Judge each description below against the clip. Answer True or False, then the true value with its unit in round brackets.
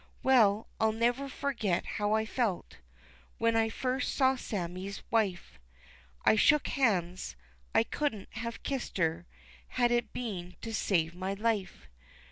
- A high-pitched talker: True (220 Hz)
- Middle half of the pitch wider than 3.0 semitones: True (4.4 semitones)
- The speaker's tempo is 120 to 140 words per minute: True (135 wpm)